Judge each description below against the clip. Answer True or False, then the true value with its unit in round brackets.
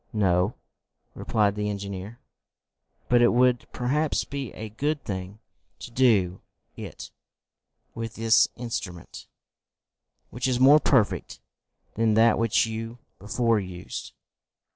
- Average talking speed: False (115 wpm)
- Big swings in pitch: False (3.2 semitones)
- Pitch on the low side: True (115 Hz)